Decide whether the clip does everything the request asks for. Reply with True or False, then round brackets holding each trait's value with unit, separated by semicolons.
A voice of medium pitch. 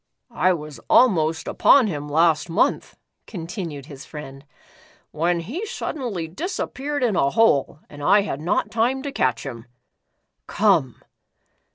True (170 Hz)